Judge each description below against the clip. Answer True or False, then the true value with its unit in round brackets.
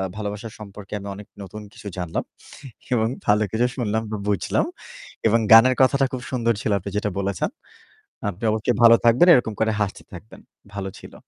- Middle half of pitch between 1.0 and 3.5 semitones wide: True (2.4 semitones)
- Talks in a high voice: False (110 Hz)